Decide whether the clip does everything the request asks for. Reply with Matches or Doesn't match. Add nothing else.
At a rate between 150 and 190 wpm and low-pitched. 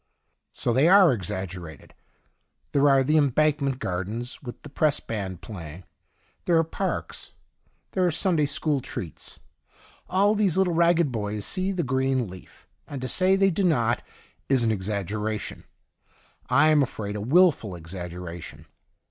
Matches